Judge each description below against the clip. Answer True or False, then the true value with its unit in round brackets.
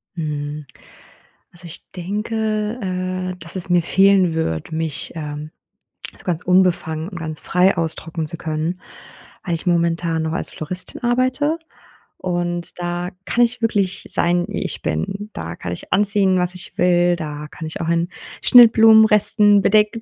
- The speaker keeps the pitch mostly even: False (3.6 semitones)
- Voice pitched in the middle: True (175 Hz)